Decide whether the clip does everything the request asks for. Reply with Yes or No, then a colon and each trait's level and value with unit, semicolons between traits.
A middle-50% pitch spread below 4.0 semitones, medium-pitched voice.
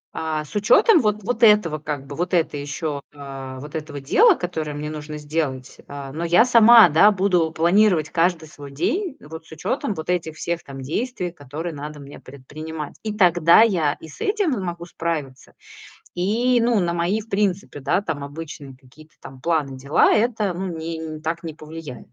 No: average, 4.6 semitones; medium, 160 Hz